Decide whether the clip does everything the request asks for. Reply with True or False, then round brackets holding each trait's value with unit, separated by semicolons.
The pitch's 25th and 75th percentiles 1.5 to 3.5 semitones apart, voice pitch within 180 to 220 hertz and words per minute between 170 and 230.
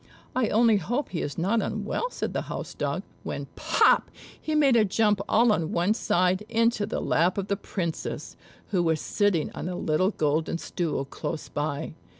False (5.2 semitones; 185 Hz; 180 wpm)